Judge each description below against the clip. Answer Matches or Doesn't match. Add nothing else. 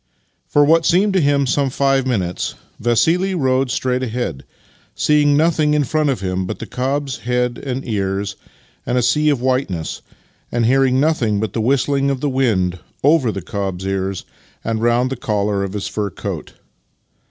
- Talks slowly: Doesn't match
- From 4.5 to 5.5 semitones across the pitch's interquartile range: Matches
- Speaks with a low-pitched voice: Matches